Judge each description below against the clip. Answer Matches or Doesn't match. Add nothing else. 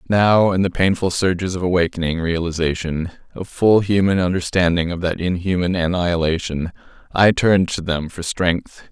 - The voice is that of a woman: Doesn't match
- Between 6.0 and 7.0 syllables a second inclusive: Doesn't match